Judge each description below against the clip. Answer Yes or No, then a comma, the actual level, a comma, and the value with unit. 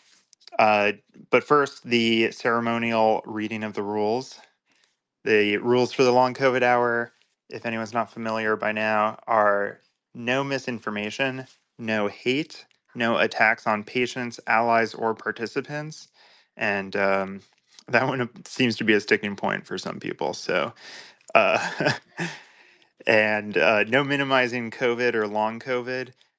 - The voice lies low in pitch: Yes, low, 115 Hz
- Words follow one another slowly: Yes, slow, 130 wpm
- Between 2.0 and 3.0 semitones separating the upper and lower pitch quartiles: Yes, narrow, 2.6 semitones